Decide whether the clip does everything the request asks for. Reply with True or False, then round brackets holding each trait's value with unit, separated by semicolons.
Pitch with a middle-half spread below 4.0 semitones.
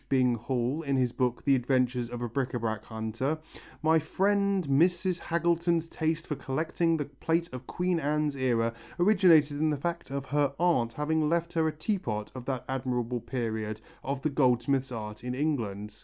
False (4.9 semitones)